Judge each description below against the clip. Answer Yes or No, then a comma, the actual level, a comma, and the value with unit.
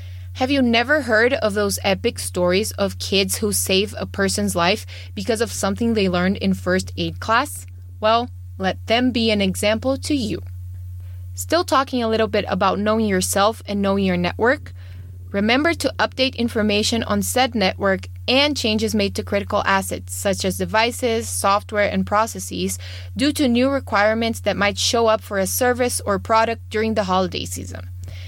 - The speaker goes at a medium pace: Yes, average, 170 wpm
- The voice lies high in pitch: Yes, high, 195 Hz